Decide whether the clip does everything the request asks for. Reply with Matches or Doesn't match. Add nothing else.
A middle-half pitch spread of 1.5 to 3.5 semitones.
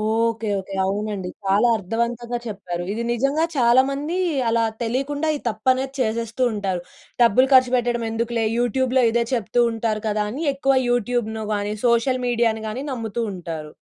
Matches